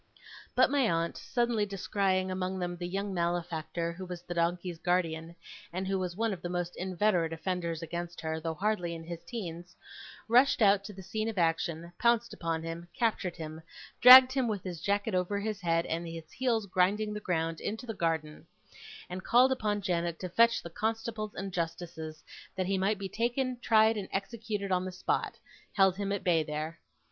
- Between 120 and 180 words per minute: No, average, 190 wpm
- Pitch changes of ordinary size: Yes, average, 3.8 semitones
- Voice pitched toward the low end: No, medium, 185 Hz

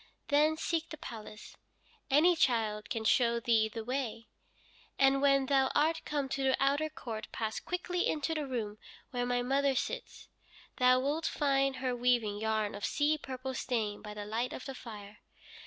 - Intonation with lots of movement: No, average, 4.2 semitones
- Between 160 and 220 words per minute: Yes, average, 170 wpm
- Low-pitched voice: No, very high, 255 Hz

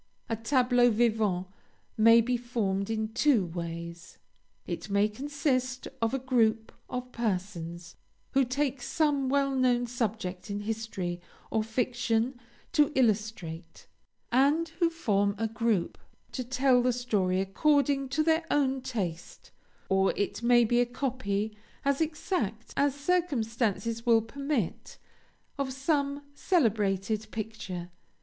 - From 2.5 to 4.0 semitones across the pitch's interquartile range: No, average, 4.4 semitones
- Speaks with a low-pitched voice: No, high, 235 Hz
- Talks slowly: Yes, slow, 125 wpm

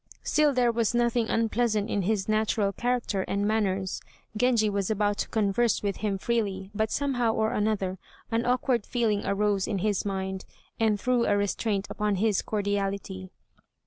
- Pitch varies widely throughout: No, narrow, 2.6 semitones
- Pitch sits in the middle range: No, high, 210 Hz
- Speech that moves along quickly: No, average, 160 wpm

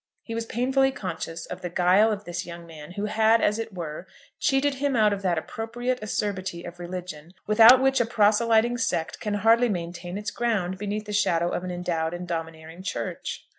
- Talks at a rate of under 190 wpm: No, average, 195 wpm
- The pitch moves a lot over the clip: No, average, 4.5 semitones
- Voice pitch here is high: Yes, high, 200 Hz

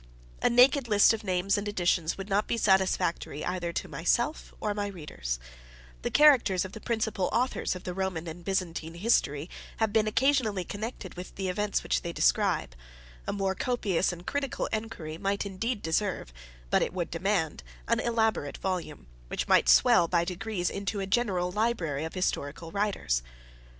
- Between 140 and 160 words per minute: No, average, 170 wpm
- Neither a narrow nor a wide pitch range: Yes, average, 4.0 semitones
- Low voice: No, high, 190 Hz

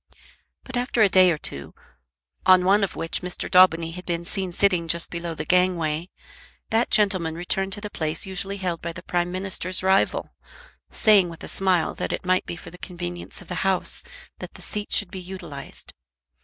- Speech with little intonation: Yes, narrow, 2.2 semitones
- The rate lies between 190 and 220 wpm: Yes, average, 195 wpm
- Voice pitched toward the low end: No, medium, 180 Hz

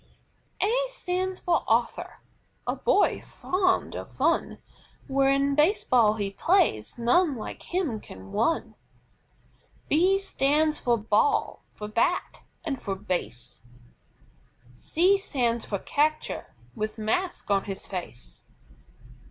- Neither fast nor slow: No, slow, 120 wpm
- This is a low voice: No, very high, 270 Hz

